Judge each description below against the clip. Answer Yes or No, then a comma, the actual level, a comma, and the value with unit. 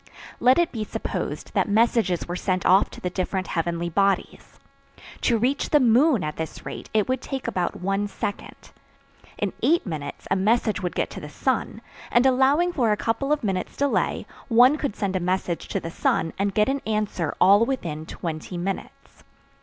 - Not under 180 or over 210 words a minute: Yes, average, 185 wpm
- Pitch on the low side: No, high, 205 Hz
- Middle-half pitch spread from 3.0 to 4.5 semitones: No, wide, 5.5 semitones